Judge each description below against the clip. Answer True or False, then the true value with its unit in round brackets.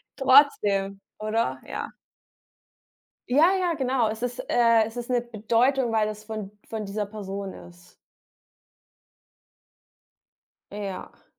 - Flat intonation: False (3.4 semitones)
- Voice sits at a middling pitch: False (220 Hz)